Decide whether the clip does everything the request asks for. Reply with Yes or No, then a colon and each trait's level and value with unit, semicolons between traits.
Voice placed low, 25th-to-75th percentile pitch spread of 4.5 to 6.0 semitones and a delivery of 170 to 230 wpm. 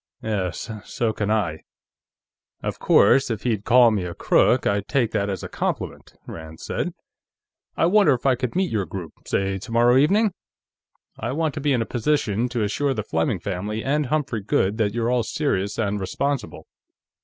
Yes: low, 115 Hz; average, 5.1 semitones; average, 180 wpm